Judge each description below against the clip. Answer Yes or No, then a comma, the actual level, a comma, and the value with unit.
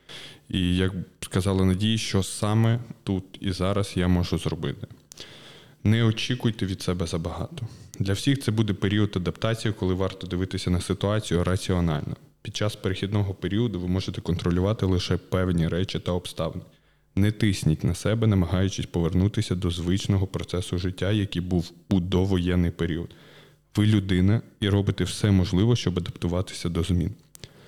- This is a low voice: Yes, very low, 95 Hz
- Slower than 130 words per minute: No, average, 145 wpm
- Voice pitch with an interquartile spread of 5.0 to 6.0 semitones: No, average, 3.1 semitones